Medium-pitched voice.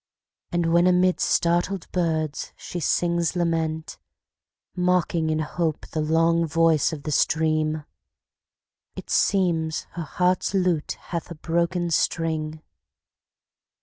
Yes: medium, 165 Hz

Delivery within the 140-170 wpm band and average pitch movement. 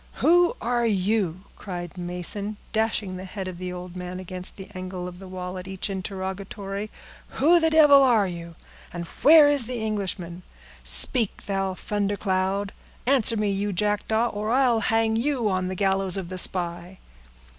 Yes: average, 165 wpm; average, 3.3 semitones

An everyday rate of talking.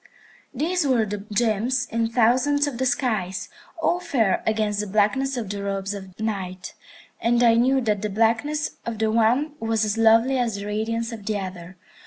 Yes: average, 185 wpm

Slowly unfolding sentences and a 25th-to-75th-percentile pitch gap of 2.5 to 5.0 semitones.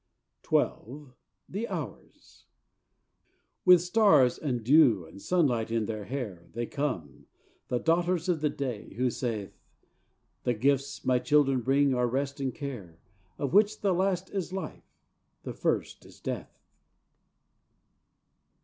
No: slow, 130 wpm; wide, 5.6 semitones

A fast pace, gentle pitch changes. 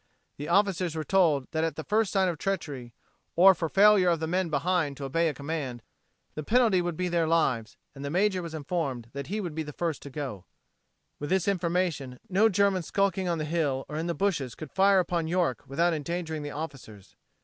No: fast, 215 wpm; average, 4.0 semitones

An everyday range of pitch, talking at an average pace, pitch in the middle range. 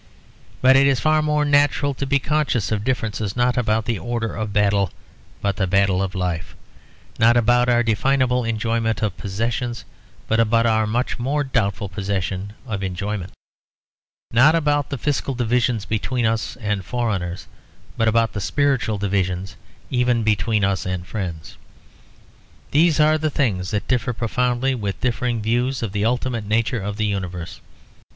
No: average, 3.8 semitones; average, 160 wpm; low, 115 Hz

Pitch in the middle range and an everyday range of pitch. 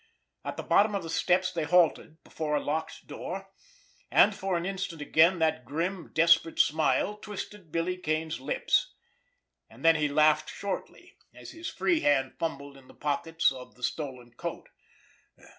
Yes: medium, 165 Hz; average, 3.8 semitones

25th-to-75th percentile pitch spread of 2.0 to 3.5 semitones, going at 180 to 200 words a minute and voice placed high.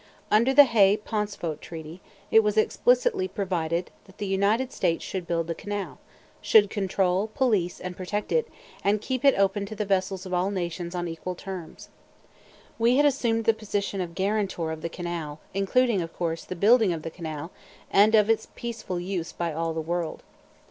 No: average, 4.0 semitones; average, 185 wpm; high, 195 Hz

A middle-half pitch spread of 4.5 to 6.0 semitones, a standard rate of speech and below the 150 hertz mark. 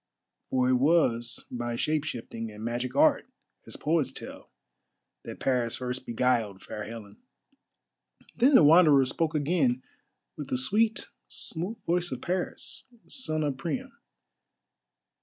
No: wide, 5.5 semitones; slow, 130 wpm; low, 135 Hz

